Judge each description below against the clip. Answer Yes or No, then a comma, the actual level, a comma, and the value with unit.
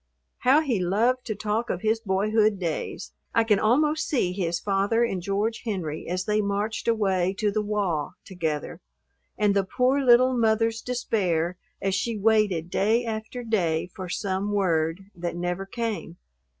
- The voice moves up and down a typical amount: Yes, average, 3.7 semitones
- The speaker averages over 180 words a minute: No, average, 160 wpm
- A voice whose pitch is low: No, high, 205 Hz